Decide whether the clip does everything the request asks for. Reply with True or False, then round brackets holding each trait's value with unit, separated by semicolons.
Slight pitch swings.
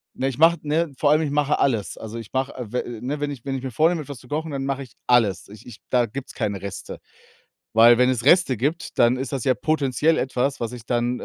False (3.5 semitones)